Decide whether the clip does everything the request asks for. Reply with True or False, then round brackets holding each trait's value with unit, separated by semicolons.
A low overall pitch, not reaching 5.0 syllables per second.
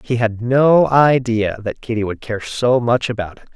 True (120 Hz; 4.5 syllables/s)